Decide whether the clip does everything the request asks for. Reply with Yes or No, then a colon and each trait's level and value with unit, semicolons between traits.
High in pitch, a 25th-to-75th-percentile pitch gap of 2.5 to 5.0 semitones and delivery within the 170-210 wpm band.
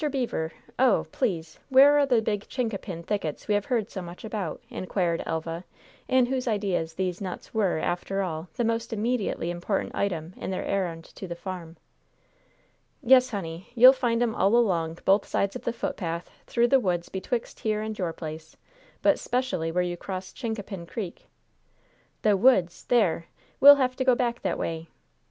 No: high, 195 Hz; wide, 5.6 semitones; average, 175 wpm